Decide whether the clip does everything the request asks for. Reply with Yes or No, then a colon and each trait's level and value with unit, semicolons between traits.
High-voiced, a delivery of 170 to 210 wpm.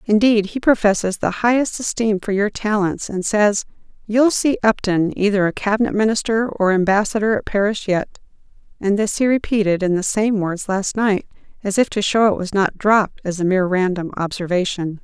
Yes: high, 205 Hz; average, 185 wpm